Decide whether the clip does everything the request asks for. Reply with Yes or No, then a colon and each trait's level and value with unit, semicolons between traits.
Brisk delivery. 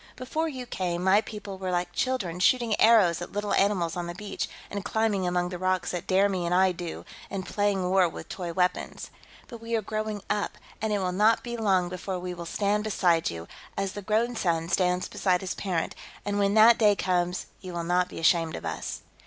Yes: fast, 220 wpm